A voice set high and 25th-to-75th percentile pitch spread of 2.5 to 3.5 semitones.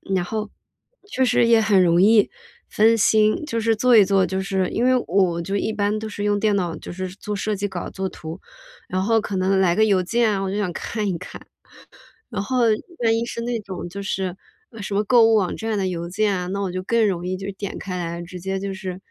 Yes: high, 200 Hz; average, 2.8 semitones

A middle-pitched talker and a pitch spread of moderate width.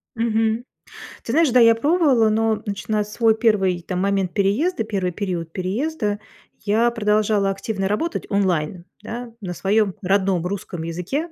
No: high, 210 Hz; average, 3.0 semitones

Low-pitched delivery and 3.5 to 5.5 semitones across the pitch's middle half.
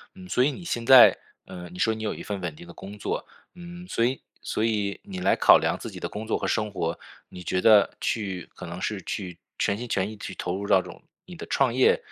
Yes: low, 105 Hz; average, 4.7 semitones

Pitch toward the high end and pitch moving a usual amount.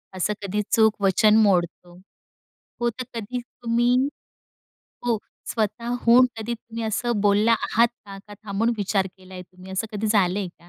Yes: high, 215 Hz; average, 3.0 semitones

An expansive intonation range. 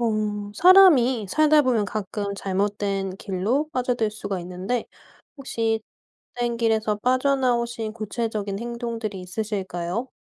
No: average, 3.3 semitones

